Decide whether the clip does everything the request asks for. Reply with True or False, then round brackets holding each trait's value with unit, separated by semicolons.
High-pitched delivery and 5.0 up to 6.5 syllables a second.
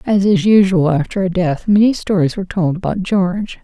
True (195 Hz; 5.4 syllables/s)